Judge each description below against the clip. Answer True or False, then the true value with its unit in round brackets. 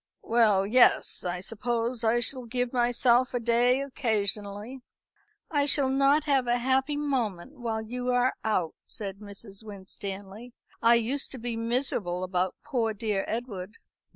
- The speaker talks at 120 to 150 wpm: True (145 wpm)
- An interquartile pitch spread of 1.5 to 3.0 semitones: False (3.6 semitones)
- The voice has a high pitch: True (235 Hz)